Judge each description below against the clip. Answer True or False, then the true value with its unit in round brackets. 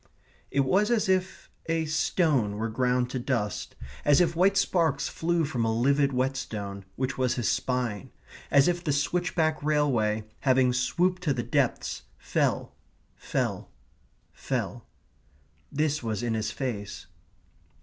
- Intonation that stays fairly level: False (5.2 semitones)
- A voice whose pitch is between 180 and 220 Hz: False (135 Hz)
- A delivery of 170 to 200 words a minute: False (140 wpm)